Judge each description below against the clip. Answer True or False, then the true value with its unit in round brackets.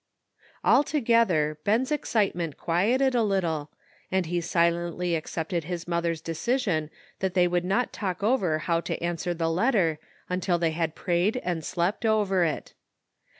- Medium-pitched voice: True (175 Hz)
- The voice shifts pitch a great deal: False (3.6 semitones)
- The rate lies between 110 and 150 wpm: True (145 wpm)